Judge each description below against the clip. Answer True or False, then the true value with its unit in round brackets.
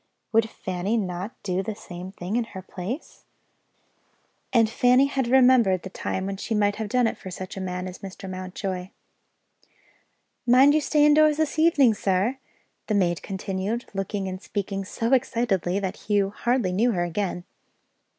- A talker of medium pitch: False (200 Hz)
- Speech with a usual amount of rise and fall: True (4.4 semitones)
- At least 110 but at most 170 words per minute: True (165 wpm)